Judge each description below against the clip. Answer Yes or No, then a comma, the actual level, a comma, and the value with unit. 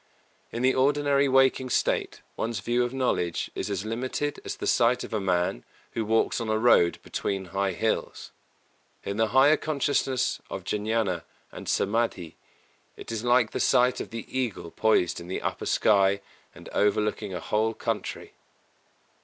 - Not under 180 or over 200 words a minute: No, average, 160 wpm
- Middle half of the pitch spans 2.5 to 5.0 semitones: Yes, average, 4.2 semitones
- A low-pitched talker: Yes, low, 110 Hz